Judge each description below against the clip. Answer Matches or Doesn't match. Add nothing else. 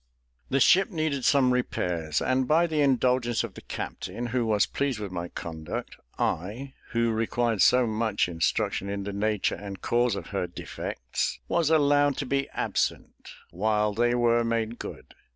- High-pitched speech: Doesn't match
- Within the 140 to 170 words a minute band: Matches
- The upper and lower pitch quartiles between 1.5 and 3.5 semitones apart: Doesn't match